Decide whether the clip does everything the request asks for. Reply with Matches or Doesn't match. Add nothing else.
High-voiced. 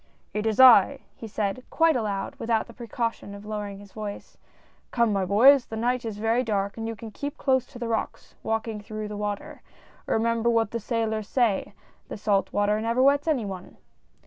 Matches